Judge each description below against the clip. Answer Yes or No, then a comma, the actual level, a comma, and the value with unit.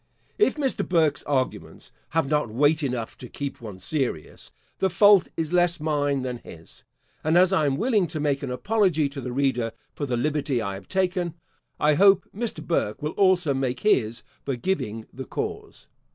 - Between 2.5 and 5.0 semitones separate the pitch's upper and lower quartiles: No, wide, 5.6 semitones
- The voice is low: No, medium, 150 Hz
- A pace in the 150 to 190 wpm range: Yes, average, 180 wpm